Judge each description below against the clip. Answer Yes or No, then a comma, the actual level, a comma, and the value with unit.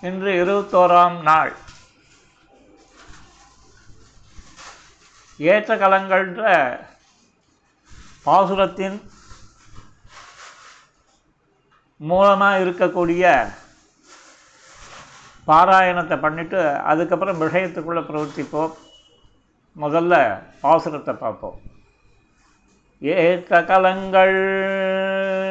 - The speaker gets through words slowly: Yes, slow, 40 wpm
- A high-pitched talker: No, medium, 180 Hz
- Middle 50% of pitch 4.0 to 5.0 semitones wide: No, average, 3.4 semitones